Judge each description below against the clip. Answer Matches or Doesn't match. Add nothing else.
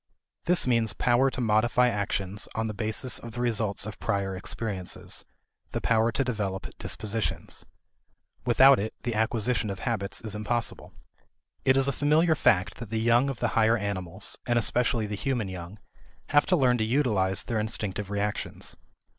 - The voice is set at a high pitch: Doesn't match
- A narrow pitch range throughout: Doesn't match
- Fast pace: Doesn't match